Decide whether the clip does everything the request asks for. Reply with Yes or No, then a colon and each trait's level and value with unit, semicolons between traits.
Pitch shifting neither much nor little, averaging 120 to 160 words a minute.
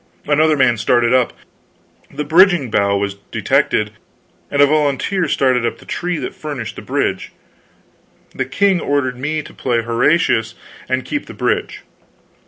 Yes: average, 4.4 semitones; average, 150 wpm